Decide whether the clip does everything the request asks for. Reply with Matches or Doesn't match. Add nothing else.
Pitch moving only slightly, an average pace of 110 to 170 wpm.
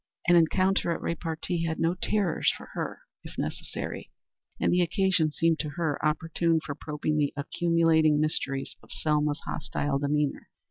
Matches